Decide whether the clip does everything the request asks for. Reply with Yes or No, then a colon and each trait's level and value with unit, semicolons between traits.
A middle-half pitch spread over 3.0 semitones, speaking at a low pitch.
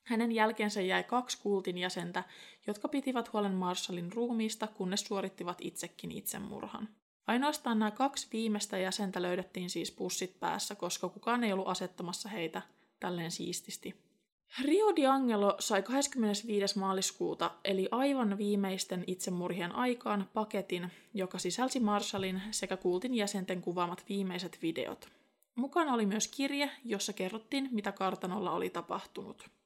No: average, 3.6 semitones; high, 205 Hz